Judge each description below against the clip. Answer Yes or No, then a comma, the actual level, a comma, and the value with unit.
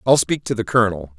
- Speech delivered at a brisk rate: Yes, fast, 255 wpm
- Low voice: Yes, low, 110 Hz